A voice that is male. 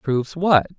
Yes: male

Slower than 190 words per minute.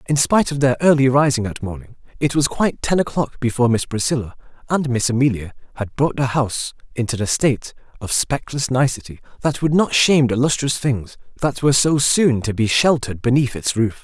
No: average, 195 wpm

